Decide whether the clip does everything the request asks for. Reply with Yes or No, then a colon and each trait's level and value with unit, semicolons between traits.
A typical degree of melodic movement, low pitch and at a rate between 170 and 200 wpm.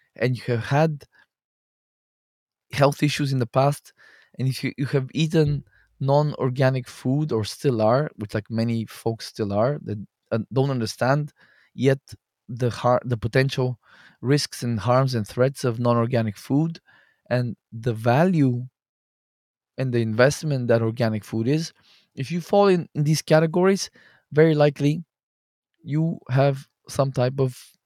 No: average, 3.6 semitones; low, 130 Hz; average, 145 wpm